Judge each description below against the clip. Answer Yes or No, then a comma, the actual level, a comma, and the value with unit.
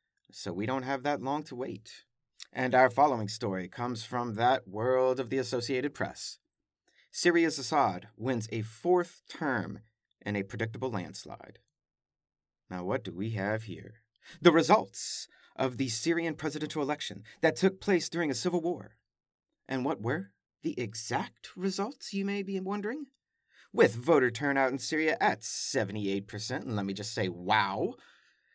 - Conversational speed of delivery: Yes, average, 155 wpm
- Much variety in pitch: Yes, wide, 6.7 semitones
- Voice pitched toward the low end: Yes, low, 130 Hz